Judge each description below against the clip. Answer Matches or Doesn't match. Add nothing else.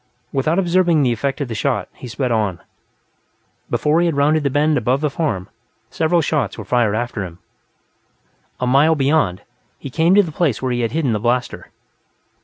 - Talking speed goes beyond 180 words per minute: Matches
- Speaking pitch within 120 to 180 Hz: Matches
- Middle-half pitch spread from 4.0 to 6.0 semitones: Matches